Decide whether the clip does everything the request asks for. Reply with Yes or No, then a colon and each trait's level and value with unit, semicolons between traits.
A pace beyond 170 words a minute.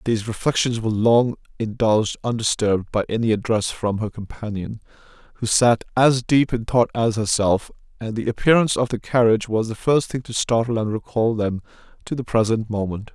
Yes: average, 180 wpm